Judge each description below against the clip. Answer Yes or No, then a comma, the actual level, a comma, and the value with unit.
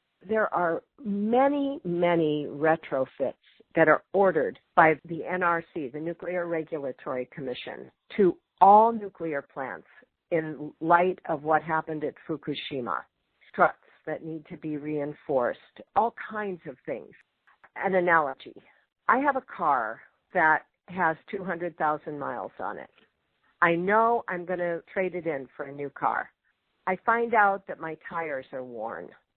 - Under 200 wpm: Yes, average, 140 wpm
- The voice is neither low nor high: Yes, medium, 170 Hz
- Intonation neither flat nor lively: Yes, average, 3.9 semitones